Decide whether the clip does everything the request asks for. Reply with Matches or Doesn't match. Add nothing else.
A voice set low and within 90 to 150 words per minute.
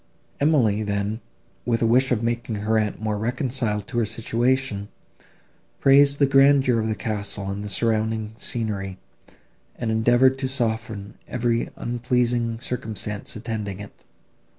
Matches